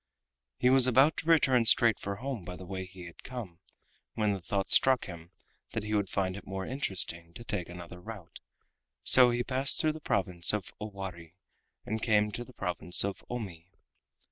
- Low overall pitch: Yes, low, 100 Hz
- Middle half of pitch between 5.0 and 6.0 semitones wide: Yes, average, 5.3 semitones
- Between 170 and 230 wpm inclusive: Yes, average, 190 wpm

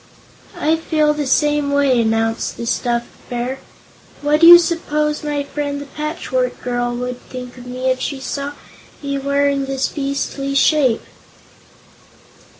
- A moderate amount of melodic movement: Yes, average, 3.0 semitones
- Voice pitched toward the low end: No, very high, 280 Hz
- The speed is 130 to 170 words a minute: Yes, average, 145 wpm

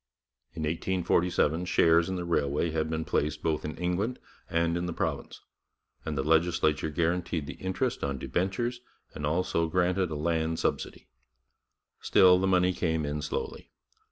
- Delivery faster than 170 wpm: No, average, 155 wpm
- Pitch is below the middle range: Yes, very low, 85 Hz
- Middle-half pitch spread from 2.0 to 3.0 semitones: Yes, narrow, 2.5 semitones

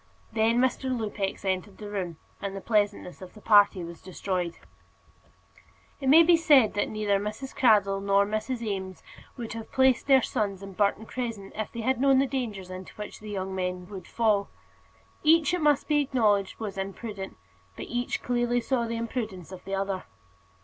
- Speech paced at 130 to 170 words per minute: No, average, 180 wpm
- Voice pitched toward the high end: Yes, high, 210 Hz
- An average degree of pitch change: Yes, average, 3.8 semitones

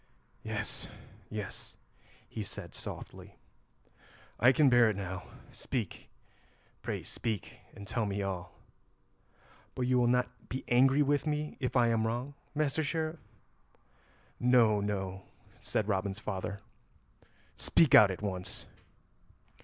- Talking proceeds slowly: Yes, slow, 120 wpm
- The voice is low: Yes, low, 115 Hz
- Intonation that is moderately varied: Yes, average, 4.6 semitones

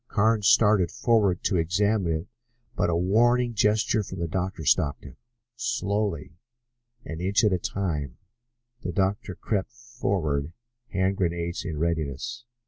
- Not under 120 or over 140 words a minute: Yes, slow, 135 wpm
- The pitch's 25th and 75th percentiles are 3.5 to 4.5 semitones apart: Yes, average, 4.2 semitones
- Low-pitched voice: Yes, very low, 95 Hz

